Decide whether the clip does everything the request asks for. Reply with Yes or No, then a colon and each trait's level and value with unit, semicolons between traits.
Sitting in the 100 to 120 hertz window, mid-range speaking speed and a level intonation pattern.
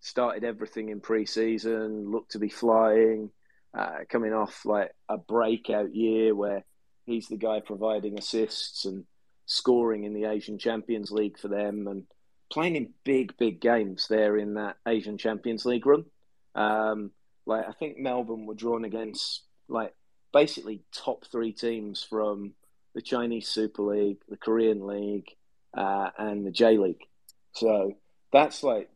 Yes: low, 110 Hz; average, 150 wpm; narrow, 1.5 semitones